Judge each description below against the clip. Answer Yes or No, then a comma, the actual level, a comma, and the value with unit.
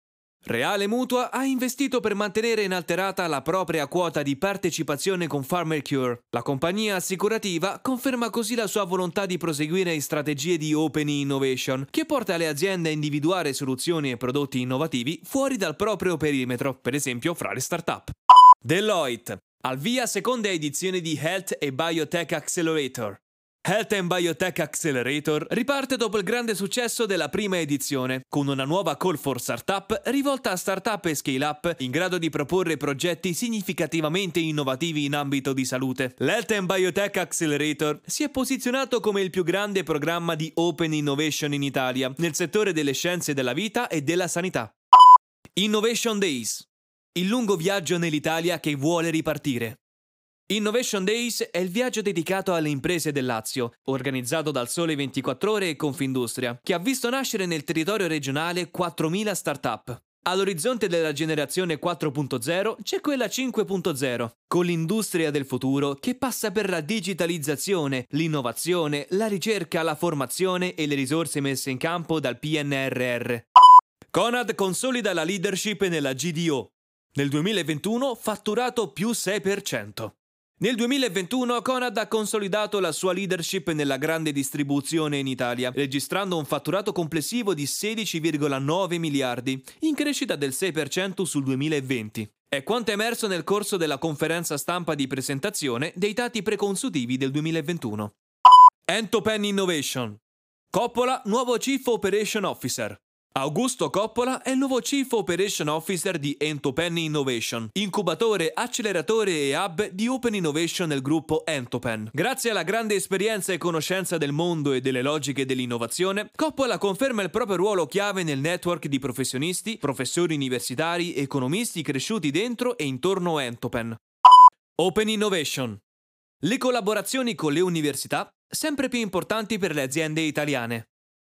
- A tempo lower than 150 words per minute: Yes, average, 140 wpm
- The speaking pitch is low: No, medium, 170 Hz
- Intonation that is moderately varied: No, wide, 6.4 semitones